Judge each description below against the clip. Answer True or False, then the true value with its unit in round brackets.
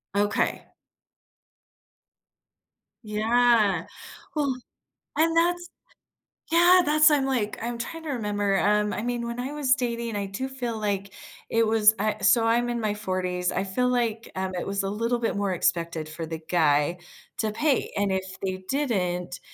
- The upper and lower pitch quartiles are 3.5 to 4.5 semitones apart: True (4.1 semitones)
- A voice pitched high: True (215 Hz)